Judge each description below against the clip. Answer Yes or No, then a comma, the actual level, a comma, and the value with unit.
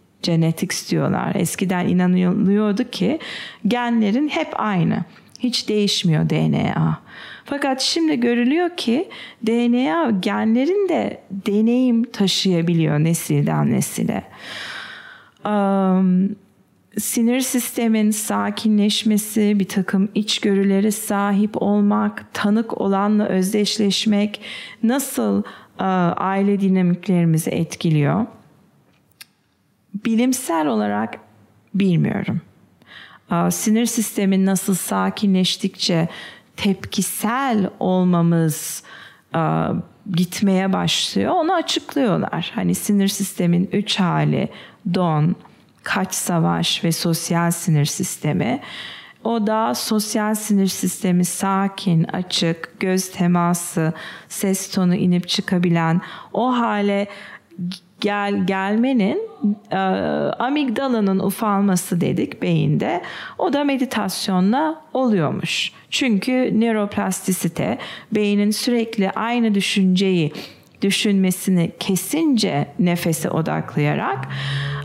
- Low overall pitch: No, high, 200 Hz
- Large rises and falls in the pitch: No, average, 3.7 semitones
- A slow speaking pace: Yes, slow, 80 wpm